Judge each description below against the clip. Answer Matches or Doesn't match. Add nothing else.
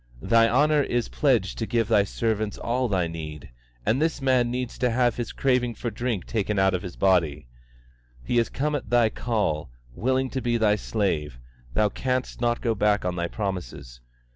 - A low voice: Matches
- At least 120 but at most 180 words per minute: Doesn't match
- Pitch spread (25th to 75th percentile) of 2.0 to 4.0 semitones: Doesn't match